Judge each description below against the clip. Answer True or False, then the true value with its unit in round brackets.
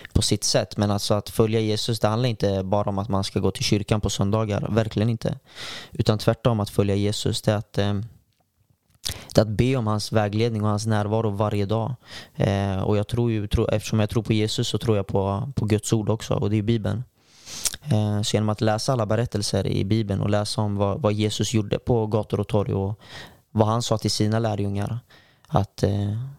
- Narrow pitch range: True (1.7 semitones)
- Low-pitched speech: True (105 Hz)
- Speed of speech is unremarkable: False (220 wpm)